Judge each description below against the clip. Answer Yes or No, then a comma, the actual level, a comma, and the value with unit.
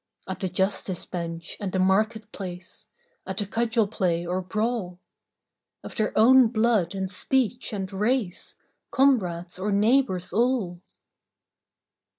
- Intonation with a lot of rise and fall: No, average, 3.8 semitones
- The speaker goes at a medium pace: No, slow, 130 wpm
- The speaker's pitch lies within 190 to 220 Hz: Yes, high, 200 Hz